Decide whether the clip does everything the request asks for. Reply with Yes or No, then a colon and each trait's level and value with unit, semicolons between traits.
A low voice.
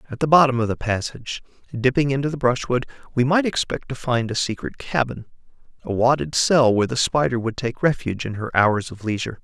Yes: low, 125 Hz